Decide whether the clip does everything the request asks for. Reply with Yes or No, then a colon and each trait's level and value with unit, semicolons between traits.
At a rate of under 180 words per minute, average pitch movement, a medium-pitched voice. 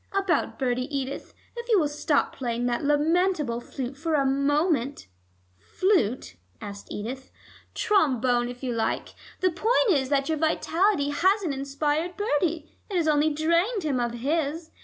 No: average, 155 wpm; average, 4.6 semitones; very high, 290 Hz